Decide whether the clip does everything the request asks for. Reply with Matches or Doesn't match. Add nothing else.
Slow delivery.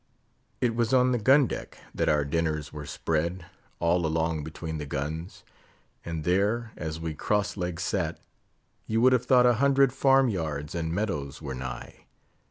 Doesn't match